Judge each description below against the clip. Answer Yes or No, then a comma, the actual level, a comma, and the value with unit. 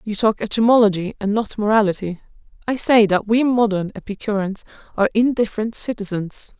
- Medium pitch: No, high, 210 Hz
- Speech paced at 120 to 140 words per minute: Yes, slow, 135 wpm